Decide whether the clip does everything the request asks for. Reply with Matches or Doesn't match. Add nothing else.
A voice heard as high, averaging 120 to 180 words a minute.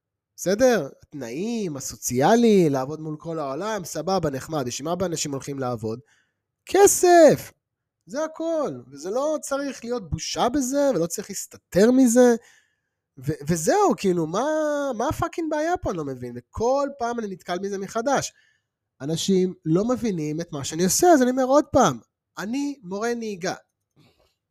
Matches